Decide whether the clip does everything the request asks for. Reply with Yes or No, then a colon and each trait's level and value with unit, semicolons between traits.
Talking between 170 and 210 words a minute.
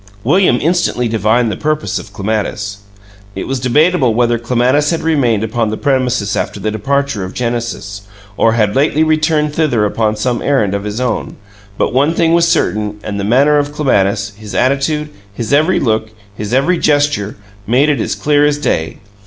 Yes: average, 175 wpm